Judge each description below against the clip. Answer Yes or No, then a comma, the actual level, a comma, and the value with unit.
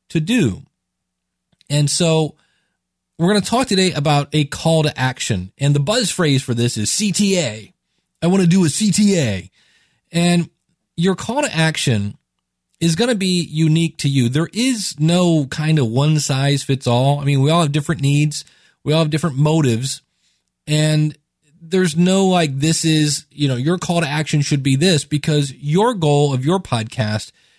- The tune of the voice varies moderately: Yes, average, 4.0 semitones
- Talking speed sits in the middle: Yes, average, 180 wpm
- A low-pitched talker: No, medium, 155 Hz